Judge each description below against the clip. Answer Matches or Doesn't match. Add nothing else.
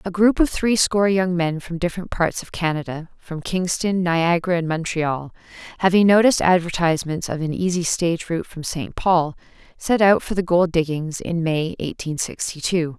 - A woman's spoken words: Matches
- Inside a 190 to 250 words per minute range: Doesn't match